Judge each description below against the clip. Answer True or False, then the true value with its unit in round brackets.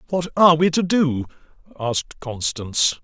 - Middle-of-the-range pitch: True (150 Hz)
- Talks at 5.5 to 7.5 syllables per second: False (4.9 syllables/s)